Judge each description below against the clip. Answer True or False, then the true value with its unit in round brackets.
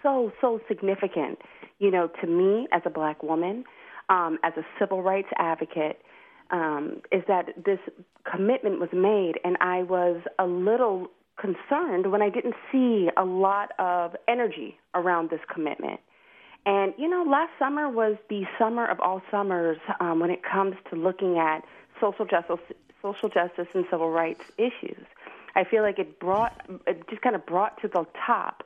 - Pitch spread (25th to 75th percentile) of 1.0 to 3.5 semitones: False (3.9 semitones)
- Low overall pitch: False (190 Hz)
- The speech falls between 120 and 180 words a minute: True (170 wpm)